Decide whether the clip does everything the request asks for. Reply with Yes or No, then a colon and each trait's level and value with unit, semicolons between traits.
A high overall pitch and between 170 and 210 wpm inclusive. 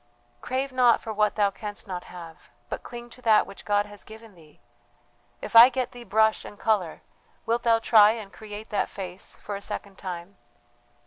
Yes: high, 210 Hz; average, 190 wpm